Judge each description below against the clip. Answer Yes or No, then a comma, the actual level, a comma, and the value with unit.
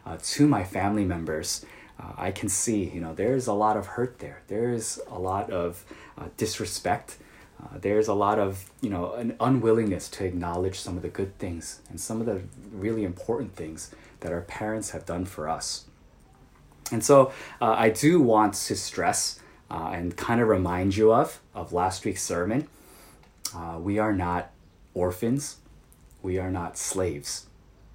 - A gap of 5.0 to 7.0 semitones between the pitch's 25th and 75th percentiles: No, average, 4.0 semitones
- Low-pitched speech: Yes, very low, 95 Hz